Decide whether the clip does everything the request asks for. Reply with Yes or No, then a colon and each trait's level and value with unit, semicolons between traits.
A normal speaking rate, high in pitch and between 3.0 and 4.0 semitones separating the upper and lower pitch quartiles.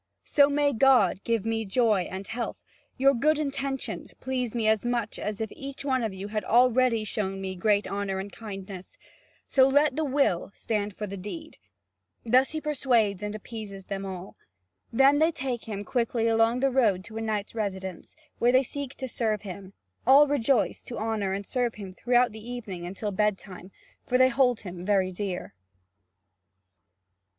No: average, 175 wpm; high, 225 Hz; average, 4.5 semitones